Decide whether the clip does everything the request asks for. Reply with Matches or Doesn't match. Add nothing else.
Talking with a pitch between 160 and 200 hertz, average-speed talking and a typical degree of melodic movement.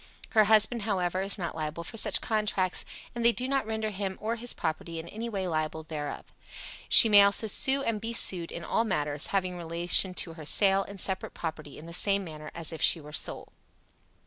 Doesn't match